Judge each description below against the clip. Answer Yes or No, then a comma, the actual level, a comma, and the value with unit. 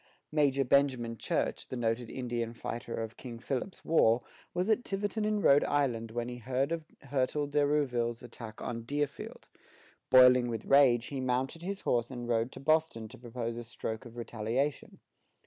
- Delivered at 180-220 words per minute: No, average, 170 wpm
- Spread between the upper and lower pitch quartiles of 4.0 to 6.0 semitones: No, average, 3.5 semitones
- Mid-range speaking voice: No, low, 125 Hz